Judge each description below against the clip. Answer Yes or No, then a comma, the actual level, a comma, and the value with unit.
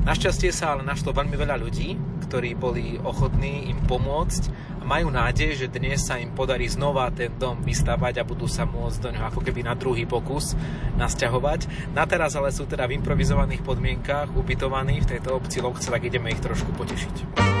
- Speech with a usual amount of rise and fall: Yes, average, 3.0 semitones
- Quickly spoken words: Yes, fast, 185 wpm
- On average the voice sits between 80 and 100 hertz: No, medium, 140 Hz